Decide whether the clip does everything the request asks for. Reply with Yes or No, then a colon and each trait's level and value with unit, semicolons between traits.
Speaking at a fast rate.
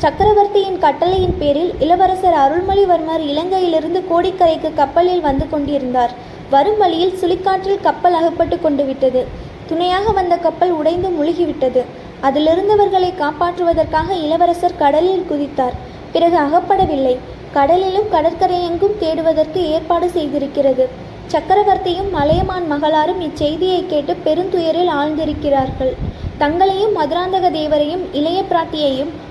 No: average, 95 wpm